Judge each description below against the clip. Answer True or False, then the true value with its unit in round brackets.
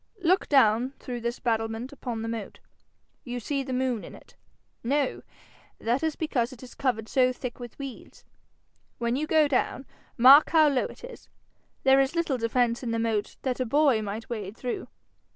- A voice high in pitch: True (250 Hz)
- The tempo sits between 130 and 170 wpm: False (185 wpm)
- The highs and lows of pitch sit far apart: False (3.0 semitones)